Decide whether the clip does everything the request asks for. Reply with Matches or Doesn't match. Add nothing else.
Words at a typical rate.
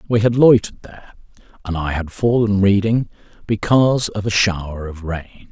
Matches